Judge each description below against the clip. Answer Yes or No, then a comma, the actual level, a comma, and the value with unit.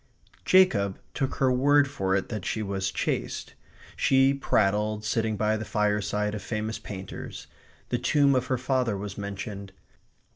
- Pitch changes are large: No, average, 4.3 semitones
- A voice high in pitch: No, low, 110 Hz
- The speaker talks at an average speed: Yes, average, 150 wpm